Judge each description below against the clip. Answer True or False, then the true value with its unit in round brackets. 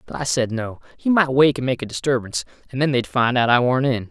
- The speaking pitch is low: True (125 Hz)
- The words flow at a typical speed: False (280 wpm)